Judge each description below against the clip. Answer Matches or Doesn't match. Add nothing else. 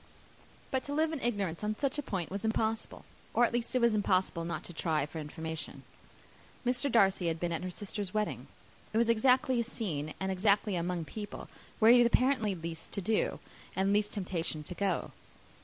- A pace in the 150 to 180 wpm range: Doesn't match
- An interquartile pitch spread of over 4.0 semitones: Matches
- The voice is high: Matches